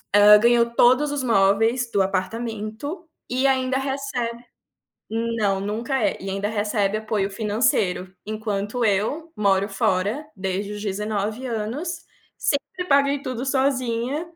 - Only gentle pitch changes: No, average, 4.3 semitones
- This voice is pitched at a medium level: No, high, 225 Hz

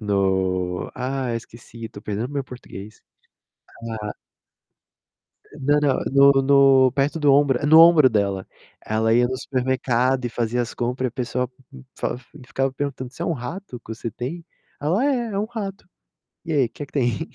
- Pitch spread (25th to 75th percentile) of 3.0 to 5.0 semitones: Yes, average, 3.6 semitones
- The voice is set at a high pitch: No, low, 130 Hz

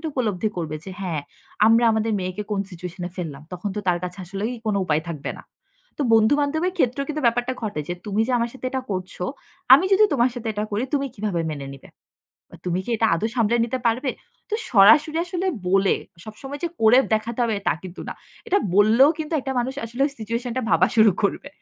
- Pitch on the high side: Yes, high, 220 Hz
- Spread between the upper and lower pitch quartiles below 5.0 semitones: No, average, 5.3 semitones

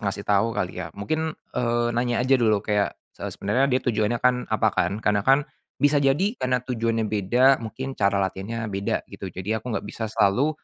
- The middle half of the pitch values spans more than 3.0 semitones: Yes, average, 4.0 semitones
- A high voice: No, low, 115 Hz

